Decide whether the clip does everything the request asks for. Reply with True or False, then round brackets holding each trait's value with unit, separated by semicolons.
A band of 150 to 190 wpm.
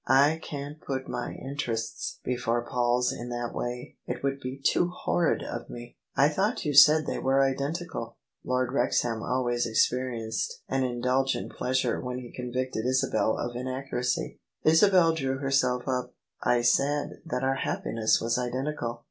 True (160 wpm)